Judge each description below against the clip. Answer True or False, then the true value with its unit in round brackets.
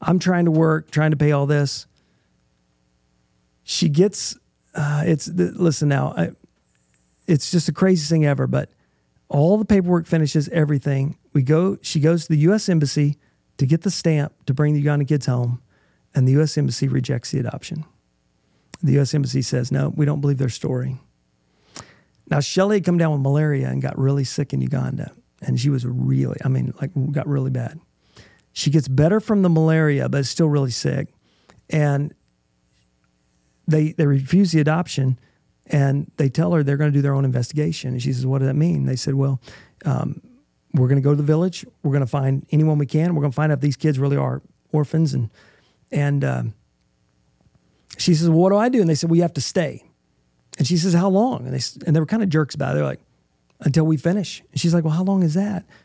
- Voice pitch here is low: False (145 Hz)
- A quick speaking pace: True (210 wpm)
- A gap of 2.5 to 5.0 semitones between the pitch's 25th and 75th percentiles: True (4.0 semitones)